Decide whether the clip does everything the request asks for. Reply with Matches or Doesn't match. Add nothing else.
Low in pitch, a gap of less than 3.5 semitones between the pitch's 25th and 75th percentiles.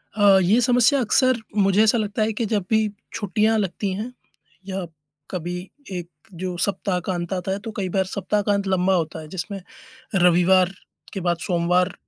Doesn't match